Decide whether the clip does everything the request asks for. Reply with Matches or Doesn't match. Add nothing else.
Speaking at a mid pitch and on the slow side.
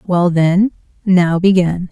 Matches